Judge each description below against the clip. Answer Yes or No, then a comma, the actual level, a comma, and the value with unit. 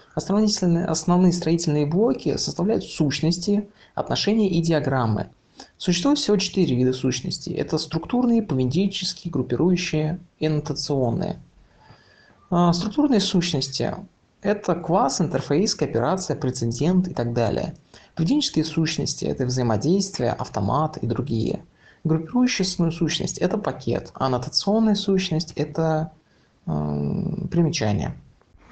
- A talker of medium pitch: Yes, medium, 165 Hz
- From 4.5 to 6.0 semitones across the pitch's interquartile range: Yes, average, 5.1 semitones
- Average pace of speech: No, slow, 95 wpm